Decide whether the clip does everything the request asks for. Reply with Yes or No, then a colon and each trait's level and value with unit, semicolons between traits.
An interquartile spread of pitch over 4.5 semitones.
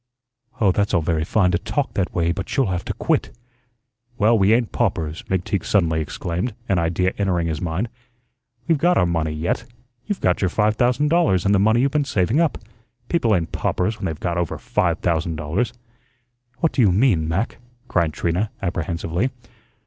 Yes: average, 5.0 semitones